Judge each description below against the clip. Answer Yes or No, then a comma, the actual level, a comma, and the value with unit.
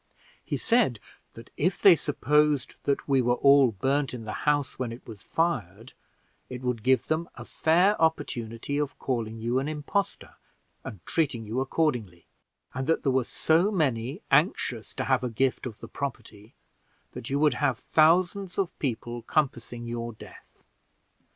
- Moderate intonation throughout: Yes, average, 4.6 semitones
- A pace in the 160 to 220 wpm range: Yes, average, 165 wpm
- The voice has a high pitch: No, low, 130 Hz